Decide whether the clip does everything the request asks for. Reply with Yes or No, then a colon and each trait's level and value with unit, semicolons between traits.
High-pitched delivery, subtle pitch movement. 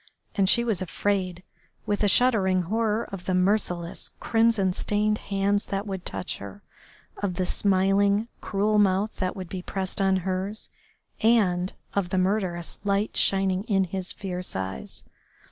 Yes: high, 195 Hz; narrow, 2.0 semitones